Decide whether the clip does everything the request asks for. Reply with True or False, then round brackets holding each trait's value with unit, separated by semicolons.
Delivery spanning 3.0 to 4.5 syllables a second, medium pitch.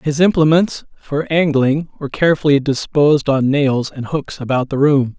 False (5.0 syllables/s; 145 Hz)